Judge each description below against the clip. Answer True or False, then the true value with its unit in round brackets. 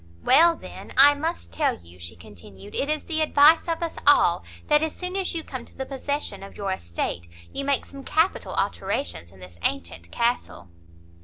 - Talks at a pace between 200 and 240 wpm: False (190 wpm)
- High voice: True (275 Hz)